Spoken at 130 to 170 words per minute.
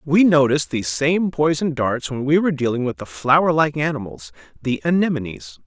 No: average, 180 wpm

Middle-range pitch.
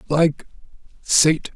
Yes: medium, 155 Hz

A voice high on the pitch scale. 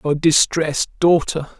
No: medium, 160 Hz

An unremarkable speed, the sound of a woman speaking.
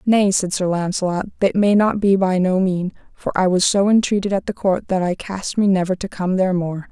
No: fast, 245 wpm; female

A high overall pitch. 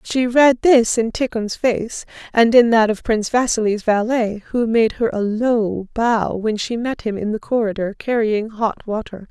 Yes: high, 225 Hz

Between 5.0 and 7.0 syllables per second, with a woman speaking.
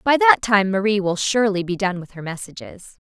Yes: 5.4 syllables/s; female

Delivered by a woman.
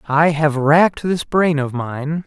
No: male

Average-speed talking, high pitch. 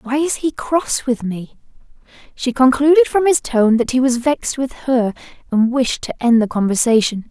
Yes: average, 190 wpm; very high, 255 Hz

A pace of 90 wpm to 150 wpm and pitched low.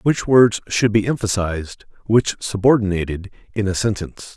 Yes: average, 140 wpm; low, 105 Hz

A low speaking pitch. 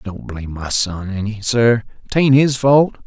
Yes: low, 115 Hz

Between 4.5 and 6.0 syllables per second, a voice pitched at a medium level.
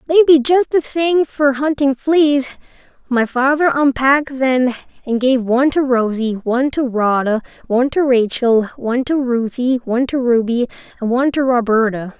No: 4.9 syllables/s; very high, 260 Hz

